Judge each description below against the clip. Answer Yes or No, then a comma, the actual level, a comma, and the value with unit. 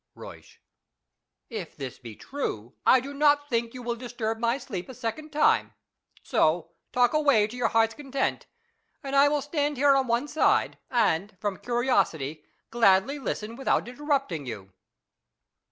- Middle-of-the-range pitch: No, high, 240 Hz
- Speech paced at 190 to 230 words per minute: No, average, 155 wpm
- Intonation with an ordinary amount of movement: No, wide, 5.8 semitones